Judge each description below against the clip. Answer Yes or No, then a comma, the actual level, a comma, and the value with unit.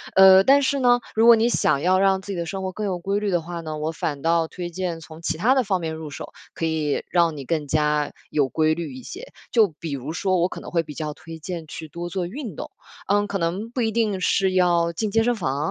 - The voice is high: No, medium, 175 Hz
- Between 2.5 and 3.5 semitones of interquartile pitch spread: No, average, 4.0 semitones